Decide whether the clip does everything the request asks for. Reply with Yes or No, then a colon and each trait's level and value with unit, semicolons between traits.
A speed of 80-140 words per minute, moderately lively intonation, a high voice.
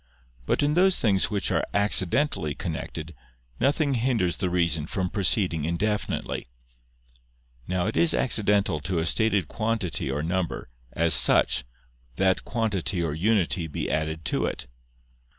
No: slow, 135 wpm; average, 4.8 semitones; very low, 95 Hz